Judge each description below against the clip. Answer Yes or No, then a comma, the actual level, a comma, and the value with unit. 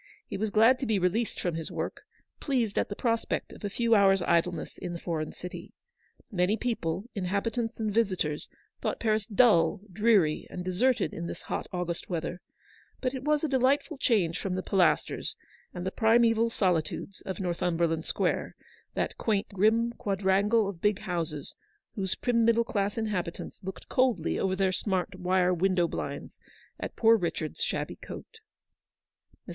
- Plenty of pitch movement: No, average, 4.3 semitones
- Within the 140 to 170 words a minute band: Yes, average, 160 wpm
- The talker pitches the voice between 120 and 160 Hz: No, high, 195 Hz